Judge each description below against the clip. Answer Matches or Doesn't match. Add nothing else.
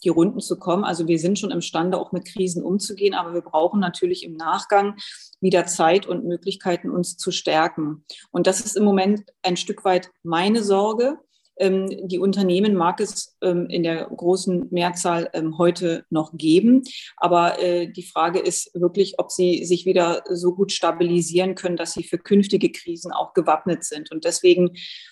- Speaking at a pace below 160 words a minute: Doesn't match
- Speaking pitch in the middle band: Matches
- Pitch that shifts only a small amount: Matches